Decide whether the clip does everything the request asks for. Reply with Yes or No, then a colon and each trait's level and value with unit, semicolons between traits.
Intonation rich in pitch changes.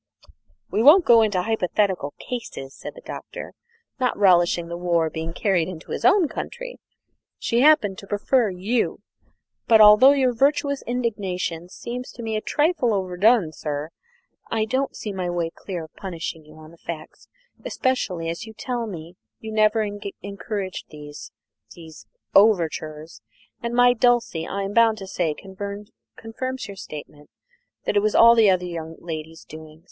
Yes: wide, 5.7 semitones